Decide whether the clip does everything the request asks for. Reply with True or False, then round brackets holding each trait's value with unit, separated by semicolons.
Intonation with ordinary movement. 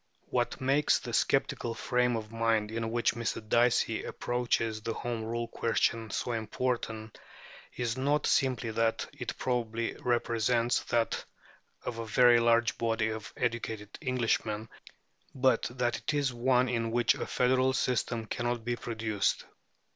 False (1.6 semitones)